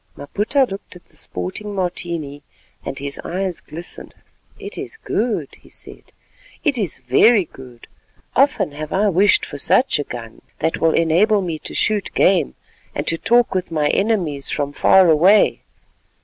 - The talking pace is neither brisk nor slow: Yes, average, 160 wpm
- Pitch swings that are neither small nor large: No, wide, 5.9 semitones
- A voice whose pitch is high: No, medium, 175 Hz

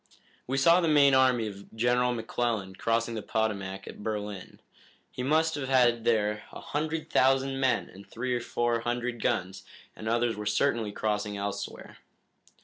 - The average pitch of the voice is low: Yes, low, 120 Hz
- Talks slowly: No, average, 160 wpm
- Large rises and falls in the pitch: No, average, 3.8 semitones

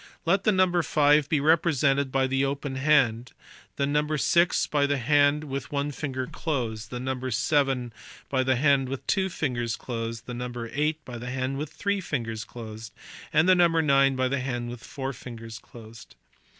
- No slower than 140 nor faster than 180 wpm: No, average, 190 wpm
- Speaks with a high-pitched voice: No, low, 135 Hz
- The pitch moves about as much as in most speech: Yes, average, 3.5 semitones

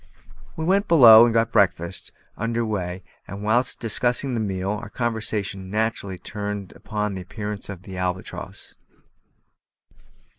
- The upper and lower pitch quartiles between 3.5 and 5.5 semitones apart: No, average, 3.1 semitones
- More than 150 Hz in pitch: No, low, 105 Hz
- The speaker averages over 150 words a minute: No, slow, 135 wpm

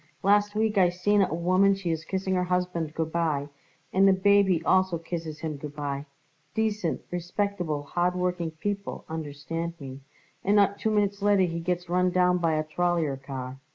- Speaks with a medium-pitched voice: Yes, medium, 175 Hz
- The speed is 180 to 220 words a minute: Yes, average, 185 wpm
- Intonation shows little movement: No, average, 3.5 semitones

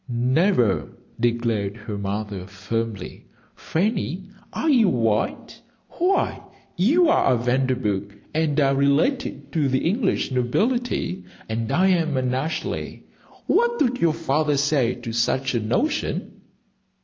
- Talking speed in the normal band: No, slow, 125 wpm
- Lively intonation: Yes, wide, 8.0 semitones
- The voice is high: No, low, 135 Hz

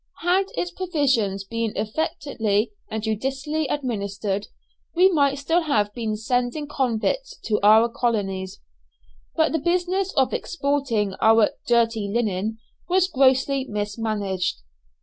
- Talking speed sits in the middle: No, slow, 115 wpm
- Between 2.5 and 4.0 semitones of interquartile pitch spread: No, wide, 5.5 semitones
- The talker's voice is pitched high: Yes, high, 235 Hz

